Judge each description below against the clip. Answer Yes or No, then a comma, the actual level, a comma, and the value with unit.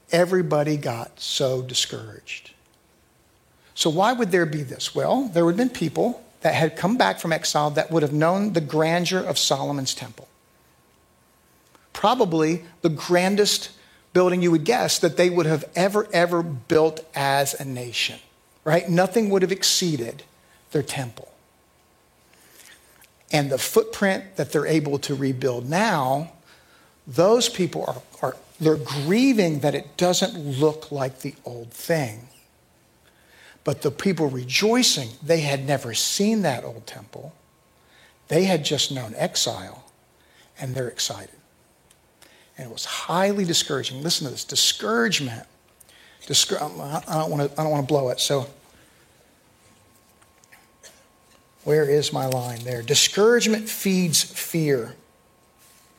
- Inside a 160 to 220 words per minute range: No, slow, 135 wpm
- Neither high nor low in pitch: Yes, medium, 155 Hz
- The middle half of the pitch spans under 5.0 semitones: Yes, average, 4.3 semitones